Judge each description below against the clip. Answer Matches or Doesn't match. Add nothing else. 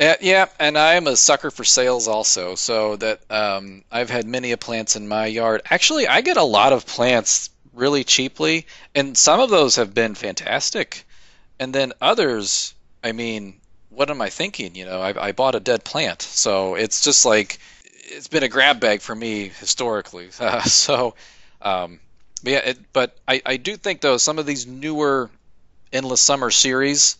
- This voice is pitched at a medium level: Doesn't match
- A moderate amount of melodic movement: Doesn't match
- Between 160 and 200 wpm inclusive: Matches